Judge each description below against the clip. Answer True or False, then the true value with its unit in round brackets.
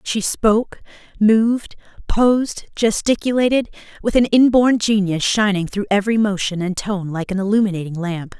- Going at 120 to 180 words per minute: True (135 wpm)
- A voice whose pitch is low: False (210 Hz)